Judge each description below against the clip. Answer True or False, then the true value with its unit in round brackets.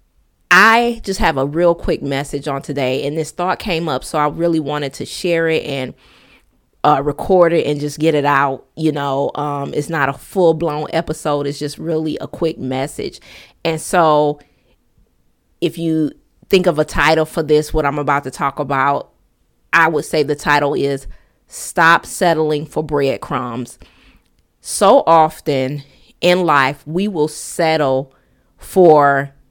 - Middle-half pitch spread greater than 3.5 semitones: False (2.8 semitones)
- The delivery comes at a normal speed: True (160 wpm)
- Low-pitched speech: False (150 Hz)